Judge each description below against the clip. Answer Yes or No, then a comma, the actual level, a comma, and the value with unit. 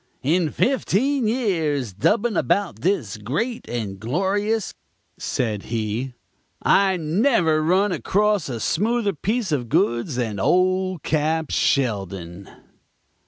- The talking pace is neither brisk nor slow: No, slow, 110 wpm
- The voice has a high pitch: No, medium, 160 Hz